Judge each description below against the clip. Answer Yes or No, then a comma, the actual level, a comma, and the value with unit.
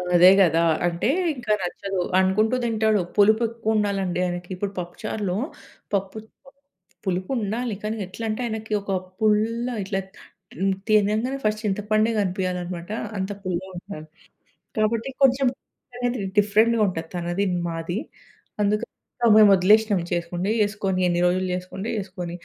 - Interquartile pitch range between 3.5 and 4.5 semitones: No, average, 3.1 semitones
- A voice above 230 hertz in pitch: No, high, 200 Hz